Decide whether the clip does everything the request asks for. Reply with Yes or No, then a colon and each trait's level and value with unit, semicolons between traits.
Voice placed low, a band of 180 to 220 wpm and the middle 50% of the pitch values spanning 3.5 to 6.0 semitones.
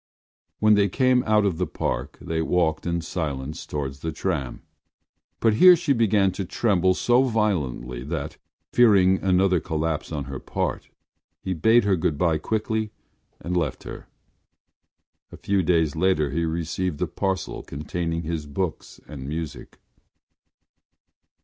No: very low, 85 Hz; average, 145 wpm; average, 4.5 semitones